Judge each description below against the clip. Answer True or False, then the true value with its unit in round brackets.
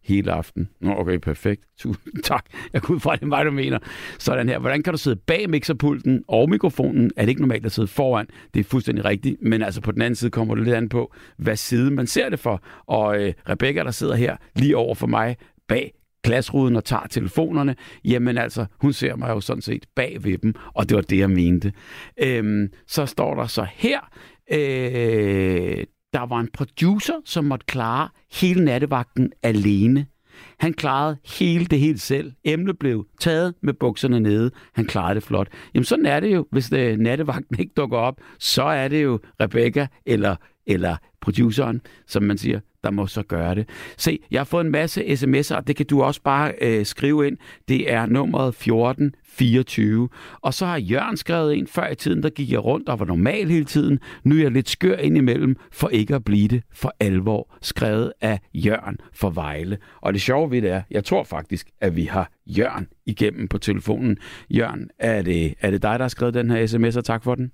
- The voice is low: True (120 Hz)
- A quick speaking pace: False (205 wpm)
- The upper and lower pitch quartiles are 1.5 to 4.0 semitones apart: False (5.1 semitones)